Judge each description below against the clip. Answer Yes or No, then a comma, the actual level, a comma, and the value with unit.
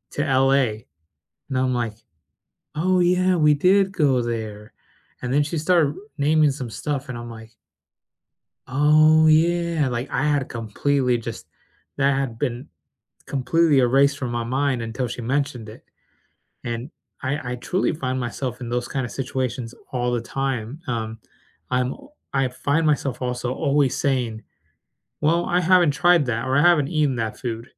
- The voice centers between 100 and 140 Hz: Yes, low, 135 Hz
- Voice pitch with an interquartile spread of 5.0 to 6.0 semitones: No, average, 3.7 semitones